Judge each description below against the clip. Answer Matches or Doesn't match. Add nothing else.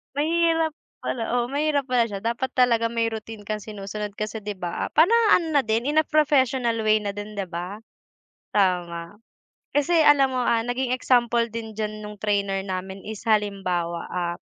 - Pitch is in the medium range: Doesn't match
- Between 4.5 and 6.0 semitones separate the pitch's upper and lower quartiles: Doesn't match